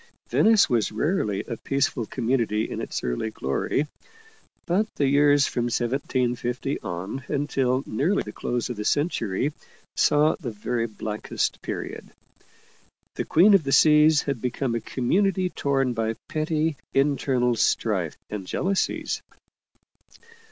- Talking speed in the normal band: No, slow, 130 wpm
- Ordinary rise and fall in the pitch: Yes, average, 4.5 semitones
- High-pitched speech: No, low, 130 Hz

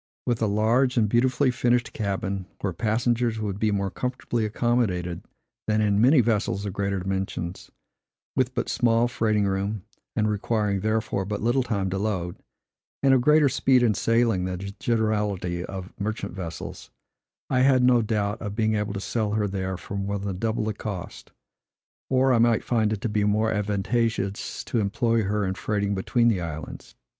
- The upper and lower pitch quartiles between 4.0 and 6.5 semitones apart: No, average, 3.1 semitones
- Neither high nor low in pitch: No, low, 105 Hz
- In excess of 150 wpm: Yes, average, 175 wpm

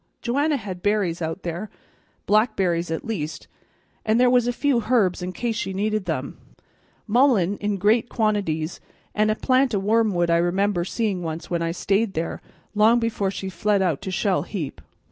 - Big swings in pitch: No, average, 4.2 semitones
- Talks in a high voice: Yes, high, 205 Hz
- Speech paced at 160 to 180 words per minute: Yes, average, 175 wpm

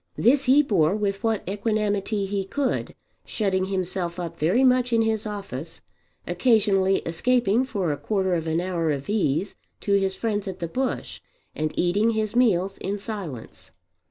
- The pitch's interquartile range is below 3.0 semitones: No, average, 3.7 semitones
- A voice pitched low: No, high, 200 Hz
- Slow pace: No, average, 160 wpm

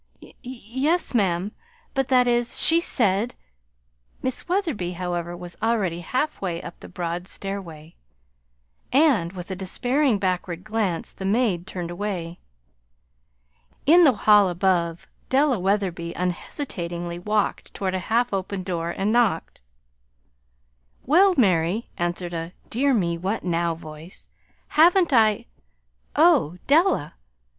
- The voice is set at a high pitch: Yes, high, 195 Hz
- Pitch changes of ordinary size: No, wide, 6.0 semitones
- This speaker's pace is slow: Yes, slow, 125 wpm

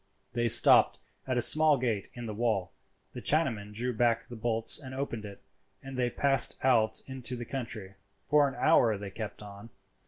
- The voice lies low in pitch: Yes, low, 120 Hz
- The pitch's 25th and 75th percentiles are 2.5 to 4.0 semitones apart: Yes, average, 3.3 semitones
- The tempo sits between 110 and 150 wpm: No, average, 185 wpm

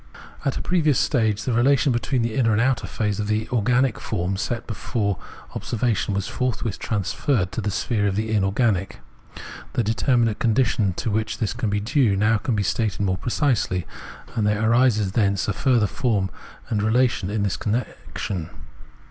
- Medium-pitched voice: No, low, 110 Hz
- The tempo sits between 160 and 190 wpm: Yes, average, 170 wpm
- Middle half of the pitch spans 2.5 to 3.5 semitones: Yes, average, 3.1 semitones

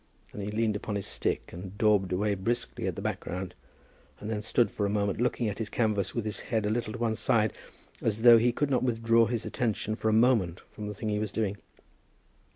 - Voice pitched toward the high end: No, low, 110 Hz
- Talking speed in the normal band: No, fast, 230 wpm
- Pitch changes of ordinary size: No, narrow, 2.1 semitones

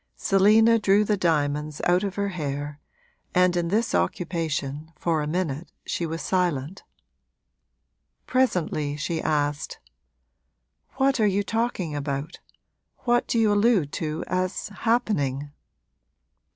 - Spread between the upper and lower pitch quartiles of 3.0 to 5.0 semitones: No, wide, 5.6 semitones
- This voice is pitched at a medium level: Yes, medium, 175 Hz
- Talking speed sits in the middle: No, slow, 120 wpm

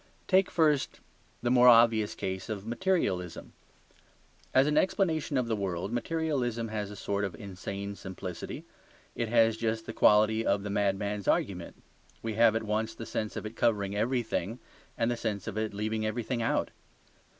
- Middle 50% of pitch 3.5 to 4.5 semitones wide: No, average, 2.9 semitones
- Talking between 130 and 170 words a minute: Yes, average, 165 wpm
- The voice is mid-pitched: No, low, 110 Hz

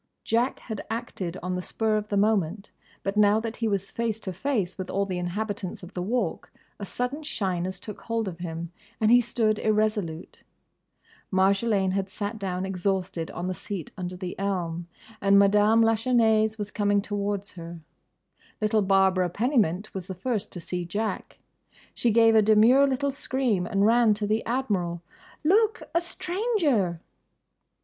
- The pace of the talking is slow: No, average, 165 wpm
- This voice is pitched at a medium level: No, high, 205 Hz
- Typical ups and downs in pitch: Yes, average, 3.4 semitones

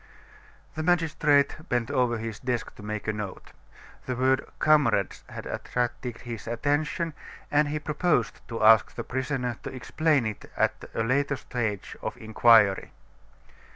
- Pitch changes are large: No, average, 4.4 semitones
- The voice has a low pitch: Yes, low, 125 Hz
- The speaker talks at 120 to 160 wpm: Yes, average, 150 wpm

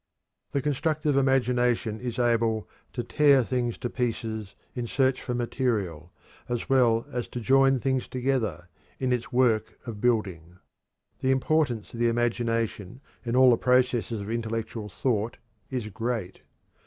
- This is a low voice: Yes, low, 120 Hz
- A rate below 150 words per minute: Yes, average, 140 wpm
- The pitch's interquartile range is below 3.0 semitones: Yes, narrow, 2.5 semitones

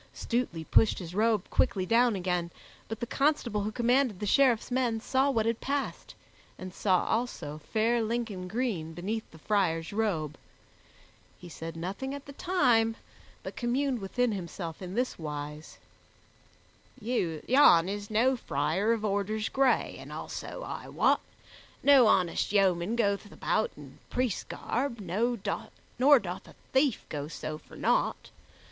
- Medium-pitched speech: No, high, 215 Hz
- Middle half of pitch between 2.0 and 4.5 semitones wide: No, average, 5.3 semitones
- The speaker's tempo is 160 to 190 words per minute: No, average, 145 wpm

